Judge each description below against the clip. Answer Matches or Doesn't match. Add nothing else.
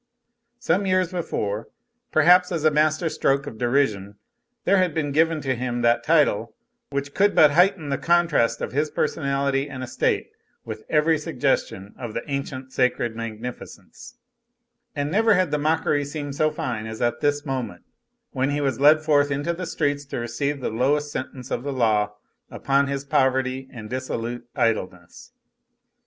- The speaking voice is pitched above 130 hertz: Matches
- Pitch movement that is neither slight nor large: Matches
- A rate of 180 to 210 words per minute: Doesn't match